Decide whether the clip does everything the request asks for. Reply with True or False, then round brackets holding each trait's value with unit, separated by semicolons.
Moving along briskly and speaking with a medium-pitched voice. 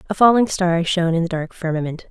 True (230 wpm; 175 Hz)